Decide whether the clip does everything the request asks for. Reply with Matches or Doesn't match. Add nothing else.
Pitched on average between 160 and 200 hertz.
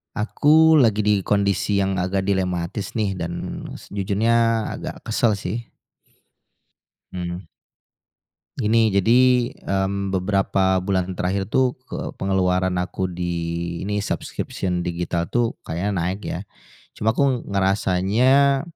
Doesn't match